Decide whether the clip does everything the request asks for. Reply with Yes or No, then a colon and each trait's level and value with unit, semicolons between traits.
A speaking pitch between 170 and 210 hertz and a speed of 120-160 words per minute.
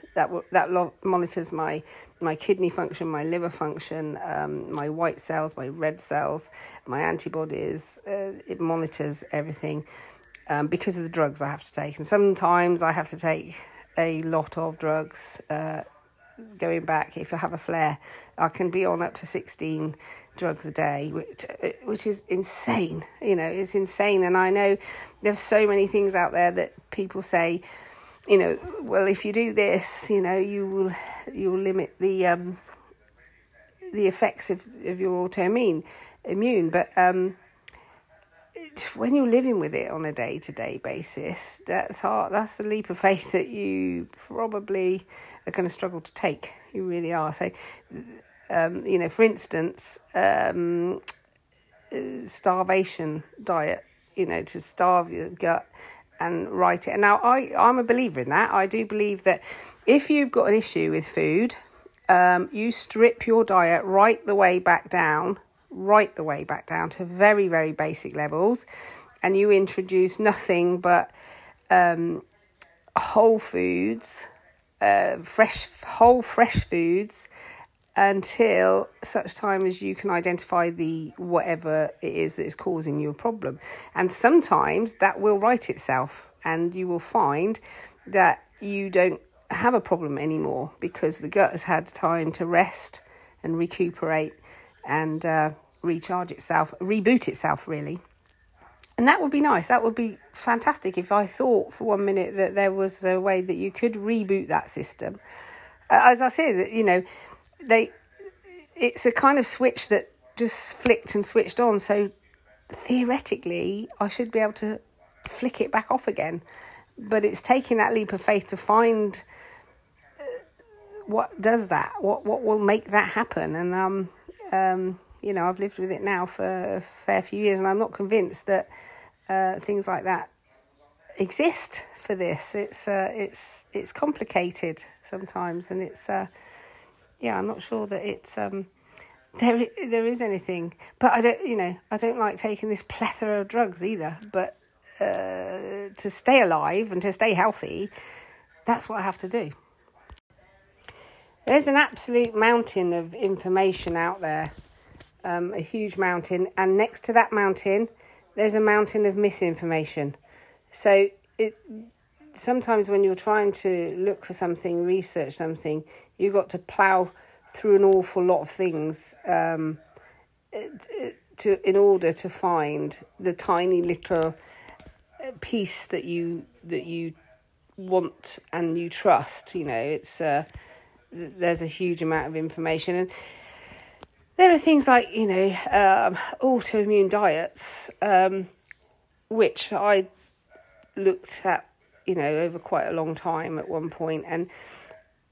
Yes: high, 190 Hz; average, 155 wpm